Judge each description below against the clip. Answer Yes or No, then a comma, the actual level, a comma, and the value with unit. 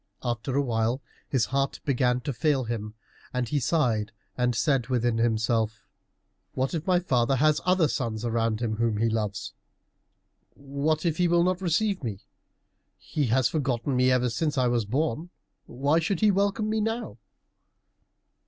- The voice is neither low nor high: No, low, 130 Hz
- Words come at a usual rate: Yes, average, 160 wpm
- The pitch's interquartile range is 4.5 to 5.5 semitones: Yes, average, 5.1 semitones